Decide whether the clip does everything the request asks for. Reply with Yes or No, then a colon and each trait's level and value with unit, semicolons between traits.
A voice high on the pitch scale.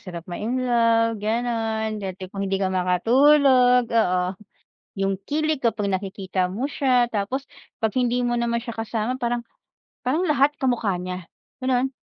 Yes: high, 230 Hz